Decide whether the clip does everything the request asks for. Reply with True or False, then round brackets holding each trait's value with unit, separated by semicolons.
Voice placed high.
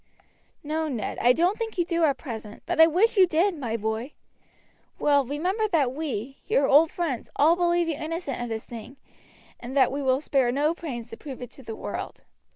True (290 Hz)